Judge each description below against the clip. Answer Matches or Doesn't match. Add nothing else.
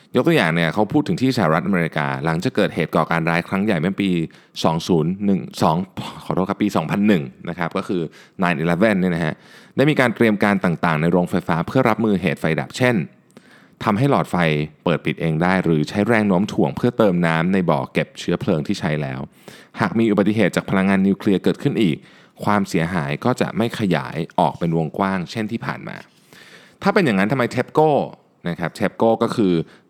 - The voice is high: Doesn't match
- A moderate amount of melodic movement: Matches